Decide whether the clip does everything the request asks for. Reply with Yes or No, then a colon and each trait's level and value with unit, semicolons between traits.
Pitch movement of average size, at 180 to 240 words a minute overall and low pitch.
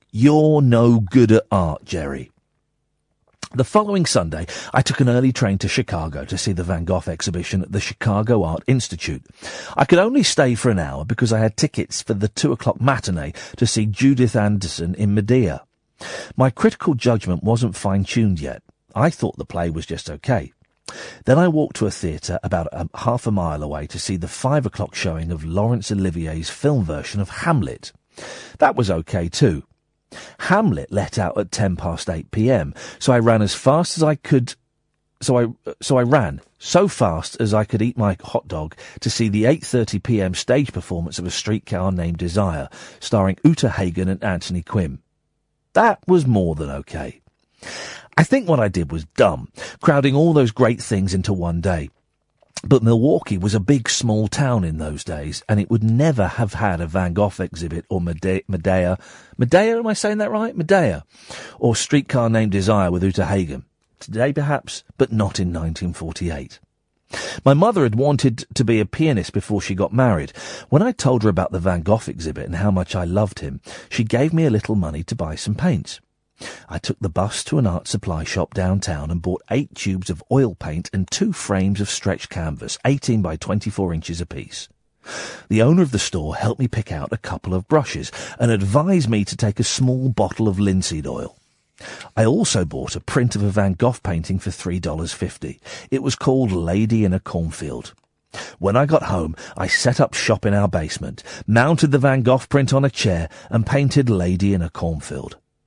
No: wide, 5.9 semitones; average, 190 wpm; low, 105 Hz